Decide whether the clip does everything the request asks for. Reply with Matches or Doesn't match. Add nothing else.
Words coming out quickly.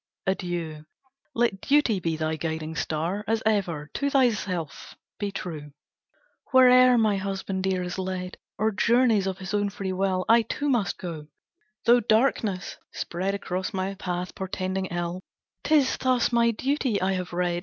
Doesn't match